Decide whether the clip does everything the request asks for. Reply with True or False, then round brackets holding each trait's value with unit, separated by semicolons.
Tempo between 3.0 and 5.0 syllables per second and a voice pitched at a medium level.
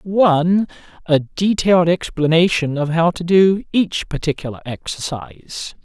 True (4.7 syllables/s; 170 Hz)